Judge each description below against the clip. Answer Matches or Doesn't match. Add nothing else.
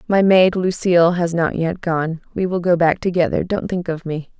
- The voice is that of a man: Doesn't match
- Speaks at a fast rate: Matches